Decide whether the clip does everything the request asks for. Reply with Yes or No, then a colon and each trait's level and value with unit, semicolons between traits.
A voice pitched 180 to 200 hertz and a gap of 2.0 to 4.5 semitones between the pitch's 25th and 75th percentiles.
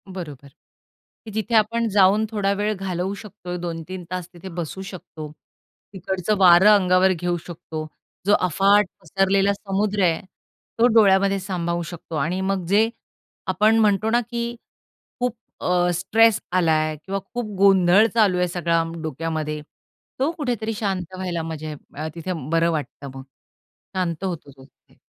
Yes: medium, 185 Hz; average, 3.5 semitones